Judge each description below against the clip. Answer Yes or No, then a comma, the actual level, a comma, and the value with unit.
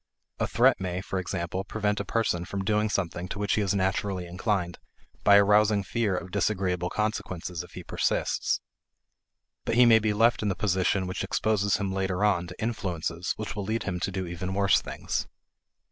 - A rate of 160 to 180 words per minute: No, average, 190 wpm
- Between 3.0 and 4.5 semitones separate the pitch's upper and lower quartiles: No, narrow, 2.6 semitones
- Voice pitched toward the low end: Yes, very low, 95 Hz